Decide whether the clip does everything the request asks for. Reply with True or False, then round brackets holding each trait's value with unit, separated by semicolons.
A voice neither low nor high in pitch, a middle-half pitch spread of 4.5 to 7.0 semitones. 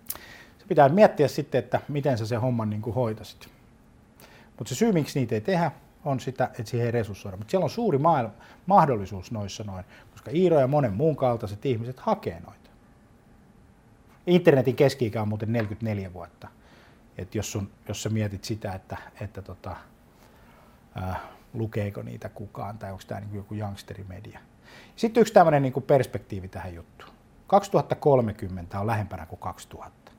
False (115 Hz; 5.1 semitones)